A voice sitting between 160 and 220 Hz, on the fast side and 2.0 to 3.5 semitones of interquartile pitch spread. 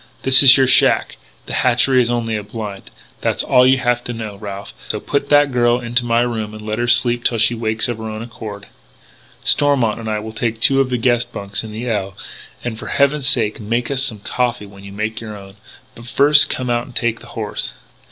No: low, 115 Hz; fast, 230 wpm; narrow, 2.6 semitones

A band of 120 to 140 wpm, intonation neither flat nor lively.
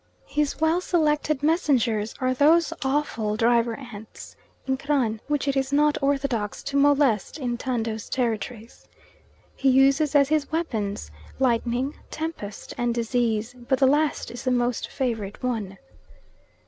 Yes: slow, 135 wpm; average, 4.0 semitones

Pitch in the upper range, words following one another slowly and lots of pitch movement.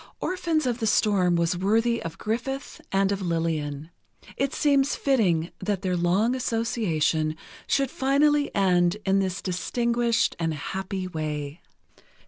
Yes: high, 195 Hz; slow, 130 wpm; wide, 5.8 semitones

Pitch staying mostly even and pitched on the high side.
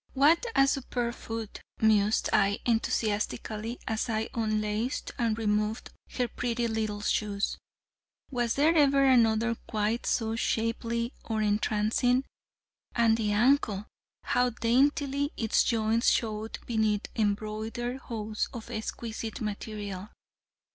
Yes: narrow, 2.1 semitones; high, 225 Hz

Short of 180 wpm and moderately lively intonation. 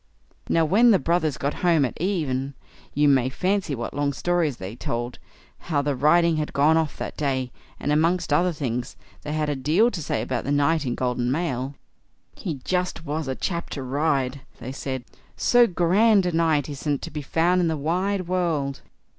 No: average, 190 wpm; average, 4.1 semitones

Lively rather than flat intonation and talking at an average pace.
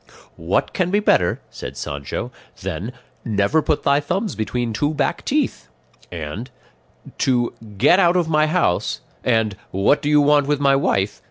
Yes: wide, 7.4 semitones; average, 160 wpm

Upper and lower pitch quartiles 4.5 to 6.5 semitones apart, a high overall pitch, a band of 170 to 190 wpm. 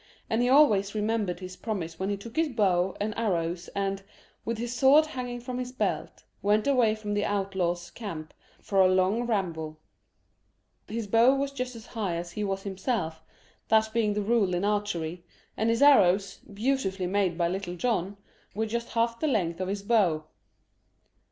No: average, 3.9 semitones; high, 205 Hz; average, 175 wpm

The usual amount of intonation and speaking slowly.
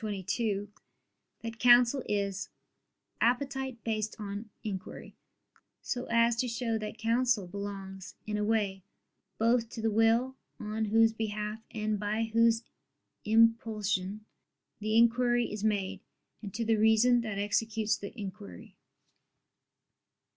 No: narrow, 1.9 semitones; slow, 125 wpm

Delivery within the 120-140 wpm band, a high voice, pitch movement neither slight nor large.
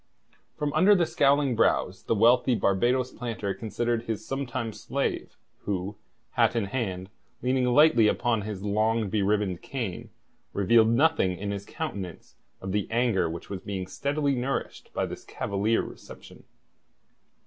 No: slow, 135 wpm; low, 110 Hz; average, 4.0 semitones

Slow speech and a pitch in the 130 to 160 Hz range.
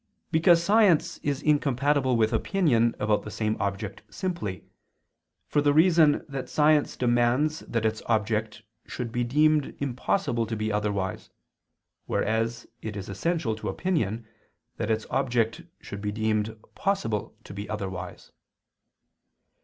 No: slow, 130 wpm; low, 115 Hz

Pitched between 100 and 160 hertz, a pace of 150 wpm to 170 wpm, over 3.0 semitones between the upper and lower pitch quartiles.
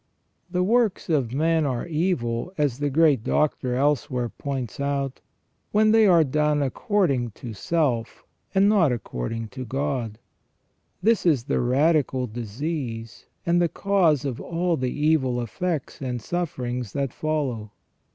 No: medium, 140 Hz; average, 140 wpm; average, 5.2 semitones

